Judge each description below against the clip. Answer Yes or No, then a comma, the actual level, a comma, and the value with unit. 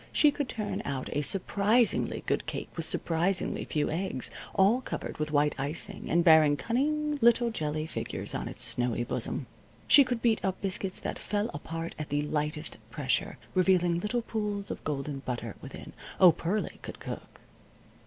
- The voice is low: No, medium, 175 Hz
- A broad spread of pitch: Yes, wide, 6.3 semitones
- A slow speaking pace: No, average, 165 wpm